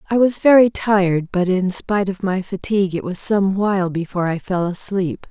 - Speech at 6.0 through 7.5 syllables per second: No, 5.3 syllables/s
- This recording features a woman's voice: Yes, female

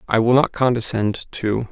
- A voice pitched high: No, low, 115 Hz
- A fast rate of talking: No, average, 175 wpm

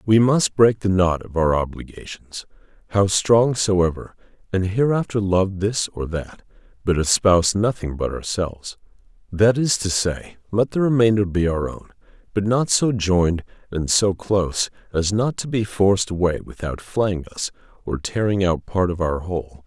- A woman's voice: No, male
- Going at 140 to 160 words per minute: No, average, 170 wpm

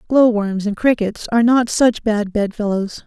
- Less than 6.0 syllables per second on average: Yes, 4.5 syllables/s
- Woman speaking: Yes, female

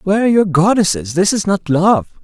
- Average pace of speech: No, fast, 215 wpm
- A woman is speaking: No, male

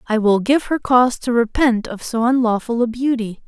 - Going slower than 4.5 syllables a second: No, 5.1 syllables/s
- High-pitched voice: Yes, high, 235 Hz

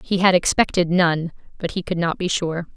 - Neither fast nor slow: No, fast, 215 wpm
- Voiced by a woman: Yes, female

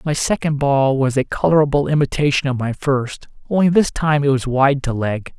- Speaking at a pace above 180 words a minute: Yes, average, 200 wpm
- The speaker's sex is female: No, male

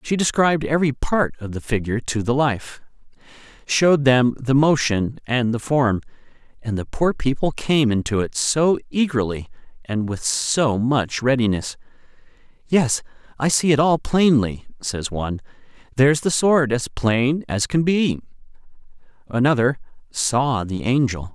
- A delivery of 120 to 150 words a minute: Yes, average, 145 wpm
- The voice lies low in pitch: Yes, low, 130 Hz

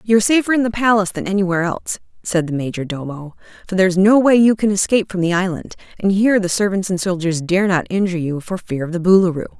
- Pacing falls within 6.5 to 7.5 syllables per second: Yes, 6.9 syllables/s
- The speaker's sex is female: Yes, female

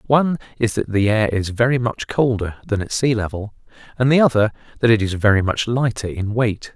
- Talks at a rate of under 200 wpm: No, fast, 205 wpm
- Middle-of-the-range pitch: No, low, 115 Hz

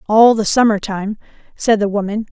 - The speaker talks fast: No, average, 175 wpm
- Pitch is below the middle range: No, high, 210 Hz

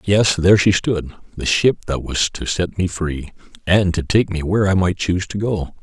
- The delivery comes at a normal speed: No, fast, 225 wpm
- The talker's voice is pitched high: No, very low, 90 Hz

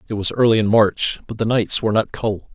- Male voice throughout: Yes, male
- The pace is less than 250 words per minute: No, fast, 260 wpm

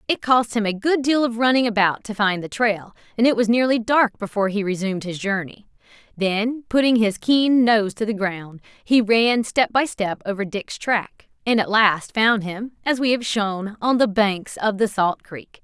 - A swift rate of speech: Yes, fast, 210 wpm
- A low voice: No, high, 215 Hz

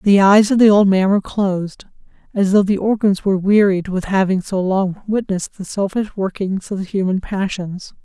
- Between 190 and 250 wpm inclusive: Yes, average, 195 wpm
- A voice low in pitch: No, high, 195 Hz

